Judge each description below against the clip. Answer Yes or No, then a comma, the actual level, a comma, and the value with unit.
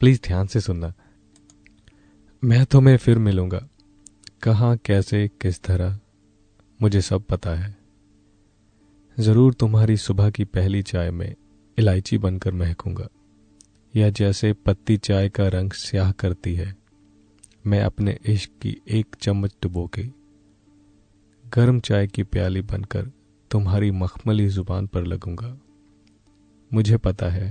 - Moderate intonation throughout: No, narrow, 1.9 semitones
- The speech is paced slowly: No, average, 125 wpm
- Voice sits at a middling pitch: No, low, 100 Hz